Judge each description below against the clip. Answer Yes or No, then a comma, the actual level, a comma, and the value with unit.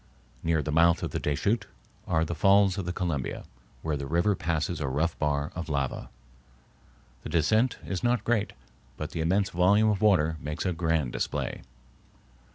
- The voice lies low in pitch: Yes, very low, 85 Hz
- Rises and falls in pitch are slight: No, average, 4.3 semitones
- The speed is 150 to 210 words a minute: Yes, average, 170 wpm